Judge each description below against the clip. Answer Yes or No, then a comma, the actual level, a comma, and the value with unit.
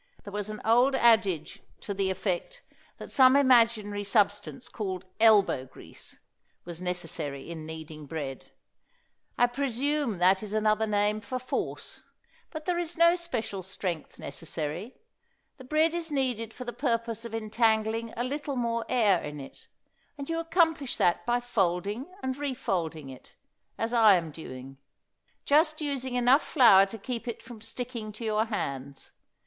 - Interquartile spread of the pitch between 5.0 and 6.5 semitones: Yes, average, 5.3 semitones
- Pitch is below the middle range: No, high, 220 Hz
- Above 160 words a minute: No, average, 155 wpm